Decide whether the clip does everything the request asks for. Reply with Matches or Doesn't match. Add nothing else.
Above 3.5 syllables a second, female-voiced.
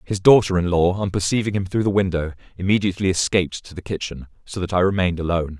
Doesn't match